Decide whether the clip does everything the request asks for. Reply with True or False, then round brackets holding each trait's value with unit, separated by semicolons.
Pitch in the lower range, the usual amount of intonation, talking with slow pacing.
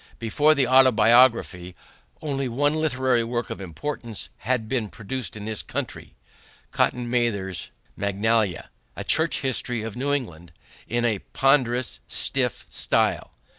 True (120 Hz; 3.5 semitones; 130 wpm)